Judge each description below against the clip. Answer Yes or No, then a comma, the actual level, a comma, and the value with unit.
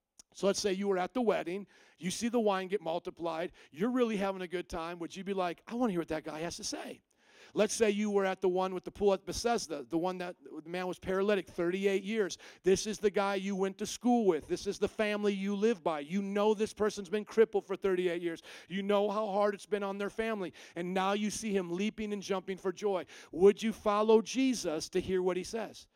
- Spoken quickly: Yes, fast, 250 wpm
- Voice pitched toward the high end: Yes, high, 195 Hz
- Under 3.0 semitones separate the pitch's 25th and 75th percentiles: Yes, narrow, 2.5 semitones